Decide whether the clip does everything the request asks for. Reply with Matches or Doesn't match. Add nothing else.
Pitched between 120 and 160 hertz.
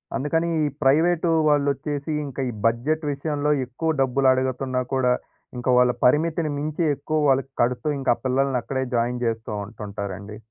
Matches